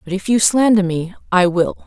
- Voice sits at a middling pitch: No, high, 195 Hz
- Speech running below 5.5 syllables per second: Yes, 5.0 syllables/s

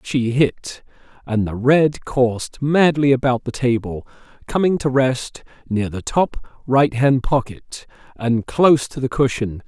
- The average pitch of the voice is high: No, low, 130 Hz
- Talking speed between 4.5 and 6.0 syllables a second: No, 3.9 syllables/s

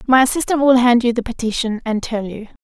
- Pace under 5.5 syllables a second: No, 6.0 syllables/s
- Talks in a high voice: Yes, high, 240 Hz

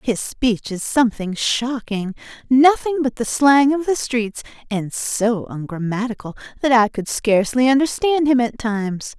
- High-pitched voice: Yes, high, 240 Hz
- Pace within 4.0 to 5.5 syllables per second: Yes, 4.4 syllables/s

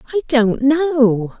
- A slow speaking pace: Yes, slow, 130 wpm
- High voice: Yes, very high, 265 Hz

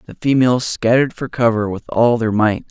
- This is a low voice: Yes, low, 115 Hz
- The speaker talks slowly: No, average, 200 wpm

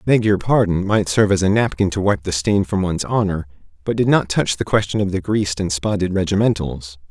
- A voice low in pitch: Yes, very low, 95 Hz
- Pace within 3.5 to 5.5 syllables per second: No, 5.8 syllables/s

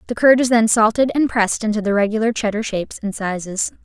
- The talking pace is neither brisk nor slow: No, fast, 220 wpm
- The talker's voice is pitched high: Yes, high, 220 Hz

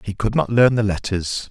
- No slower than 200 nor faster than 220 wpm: No, fast, 240 wpm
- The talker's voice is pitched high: No, low, 105 Hz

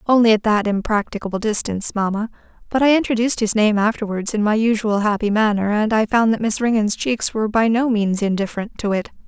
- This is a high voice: Yes, high, 215 Hz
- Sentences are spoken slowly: No, average, 200 wpm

